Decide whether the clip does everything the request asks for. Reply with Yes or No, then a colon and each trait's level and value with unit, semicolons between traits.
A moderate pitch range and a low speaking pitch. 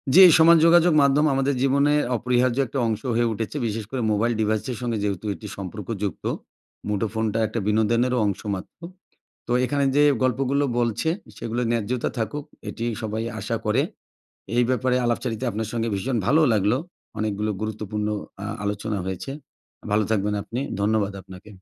Yes: average, 3.4 semitones; low, 115 Hz